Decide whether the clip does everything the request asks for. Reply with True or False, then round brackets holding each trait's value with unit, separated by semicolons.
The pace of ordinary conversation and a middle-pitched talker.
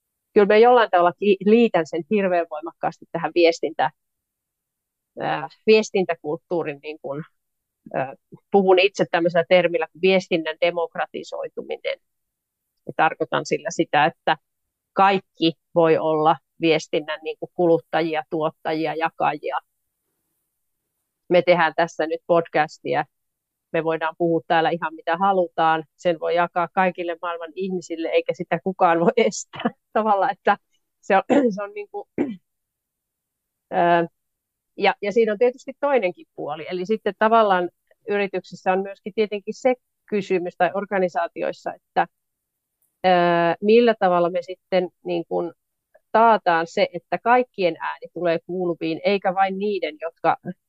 True (115 wpm; 175 Hz)